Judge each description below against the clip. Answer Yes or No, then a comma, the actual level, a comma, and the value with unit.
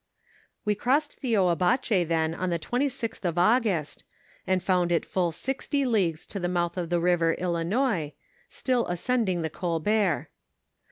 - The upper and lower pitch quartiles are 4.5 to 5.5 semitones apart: Yes, average, 5.2 semitones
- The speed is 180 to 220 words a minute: No, average, 150 wpm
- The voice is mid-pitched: Yes, medium, 180 Hz